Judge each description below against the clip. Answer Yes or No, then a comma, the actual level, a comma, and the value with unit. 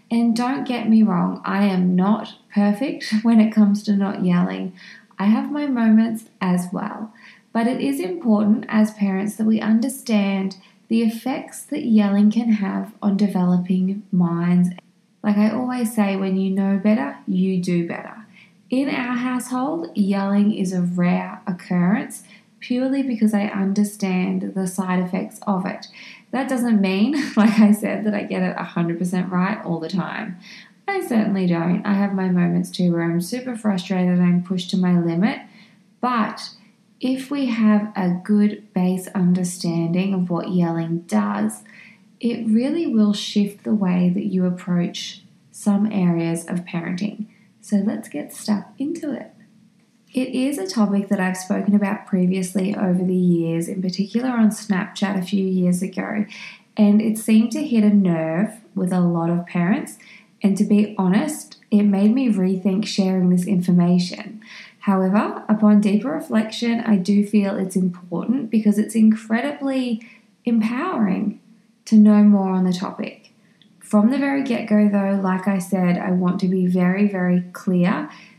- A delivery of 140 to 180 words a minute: Yes, average, 160 wpm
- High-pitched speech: Yes, high, 205 Hz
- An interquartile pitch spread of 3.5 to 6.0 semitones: No, average, 2.8 semitones